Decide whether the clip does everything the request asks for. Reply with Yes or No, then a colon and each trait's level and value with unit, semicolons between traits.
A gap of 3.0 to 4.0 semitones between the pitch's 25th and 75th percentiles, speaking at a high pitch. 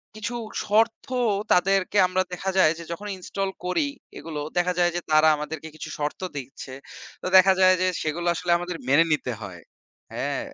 No: average, 3.6 semitones; medium, 175 Hz